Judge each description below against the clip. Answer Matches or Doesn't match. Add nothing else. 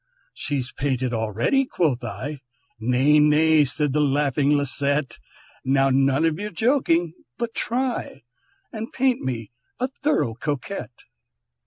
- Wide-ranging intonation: Doesn't match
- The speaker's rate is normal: Doesn't match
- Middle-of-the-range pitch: Matches